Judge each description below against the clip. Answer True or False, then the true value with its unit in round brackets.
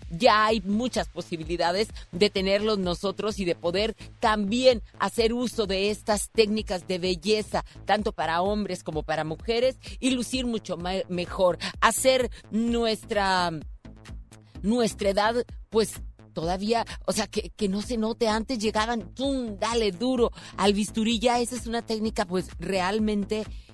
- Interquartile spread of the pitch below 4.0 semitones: True (3.6 semitones)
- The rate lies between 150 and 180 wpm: False (140 wpm)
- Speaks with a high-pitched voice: True (210 Hz)